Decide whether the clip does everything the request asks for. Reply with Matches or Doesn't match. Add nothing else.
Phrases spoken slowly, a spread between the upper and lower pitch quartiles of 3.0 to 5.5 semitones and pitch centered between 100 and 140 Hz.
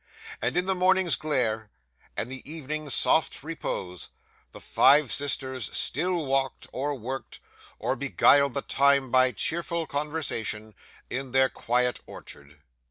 Matches